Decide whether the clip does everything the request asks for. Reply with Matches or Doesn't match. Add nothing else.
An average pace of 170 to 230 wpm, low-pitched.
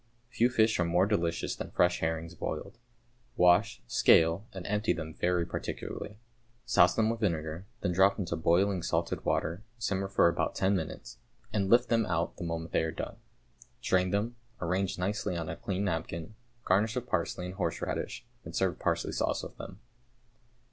Matches